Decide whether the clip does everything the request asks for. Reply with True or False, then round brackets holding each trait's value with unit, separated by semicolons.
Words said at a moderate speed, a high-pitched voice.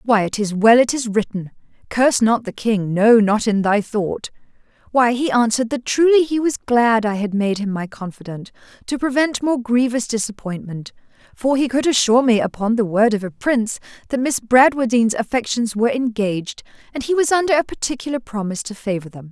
True (185 wpm; 230 Hz)